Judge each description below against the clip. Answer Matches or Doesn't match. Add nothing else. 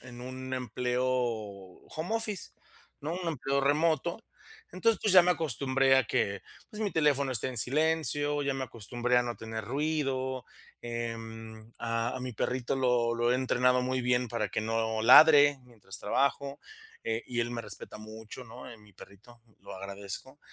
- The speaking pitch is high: Doesn't match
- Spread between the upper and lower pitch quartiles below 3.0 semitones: Doesn't match